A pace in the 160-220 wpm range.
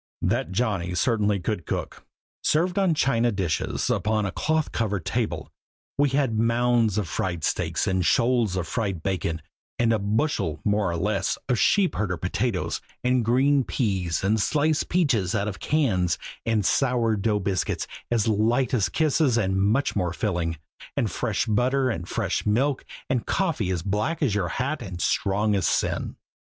Yes: average, 165 wpm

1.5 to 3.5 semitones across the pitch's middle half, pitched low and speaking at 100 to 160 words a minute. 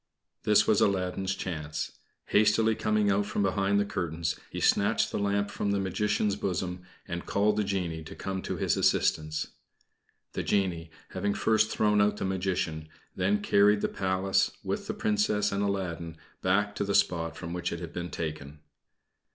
No: average, 3.0 semitones; very low, 95 Hz; average, 170 wpm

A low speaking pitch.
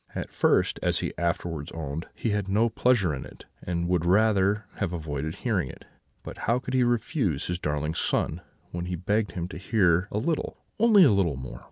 Yes: very low, 90 Hz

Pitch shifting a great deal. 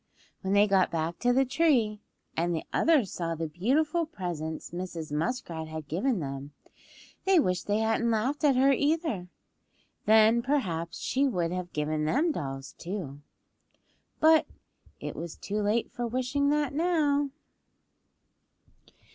Yes: wide, 8.7 semitones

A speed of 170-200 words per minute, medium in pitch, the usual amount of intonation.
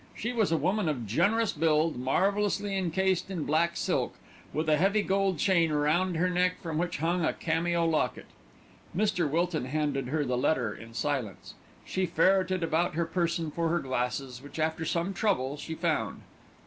Yes: average, 175 wpm; medium, 165 Hz; average, 3.8 semitones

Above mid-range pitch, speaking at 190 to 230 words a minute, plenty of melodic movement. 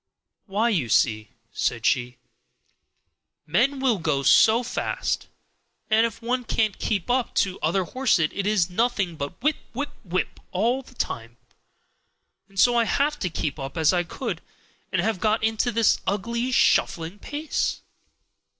No: high, 210 Hz; average, 155 wpm; wide, 6.2 semitones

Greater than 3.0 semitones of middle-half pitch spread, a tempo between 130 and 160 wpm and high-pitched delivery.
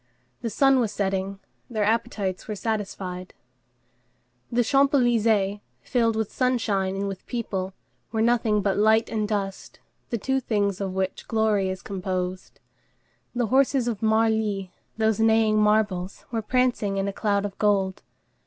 No: average, 2.7 semitones; average, 145 wpm; high, 210 Hz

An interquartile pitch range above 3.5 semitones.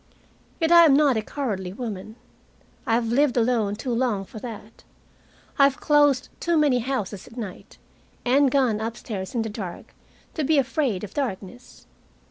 Yes: average, 4.7 semitones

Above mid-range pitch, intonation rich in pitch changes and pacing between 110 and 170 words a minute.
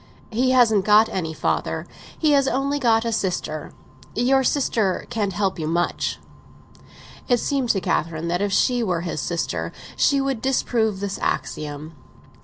Yes: high, 215 Hz; wide, 6.3 semitones; average, 150 wpm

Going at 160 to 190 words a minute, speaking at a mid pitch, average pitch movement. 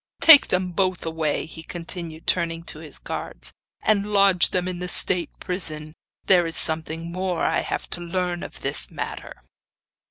No: average, 165 wpm; medium, 175 Hz; narrow, 2.1 semitones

